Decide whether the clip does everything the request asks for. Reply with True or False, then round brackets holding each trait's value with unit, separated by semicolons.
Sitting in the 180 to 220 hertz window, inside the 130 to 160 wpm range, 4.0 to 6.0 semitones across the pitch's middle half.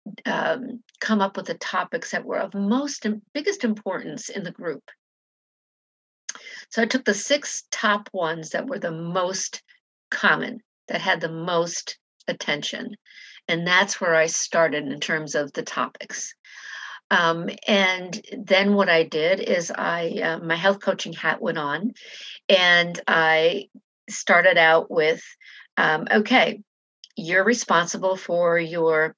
True (190 Hz; 140 wpm; 4.7 semitones)